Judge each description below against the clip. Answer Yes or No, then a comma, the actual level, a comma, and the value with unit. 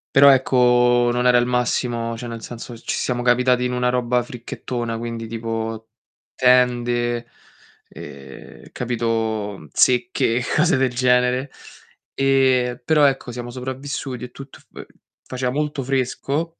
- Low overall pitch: Yes, low, 125 Hz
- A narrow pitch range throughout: Yes, narrow, 1.5 semitones